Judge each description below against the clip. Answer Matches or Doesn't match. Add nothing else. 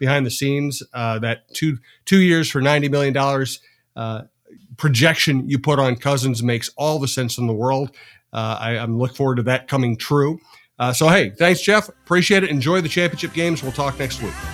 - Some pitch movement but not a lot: Matches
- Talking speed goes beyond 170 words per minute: Matches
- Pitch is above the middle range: Doesn't match